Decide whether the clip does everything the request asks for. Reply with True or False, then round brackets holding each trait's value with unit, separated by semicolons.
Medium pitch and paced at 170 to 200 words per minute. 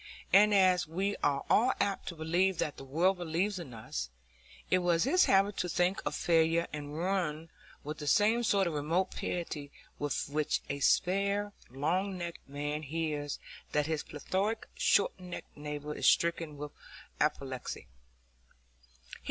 False (165 Hz; 150 wpm)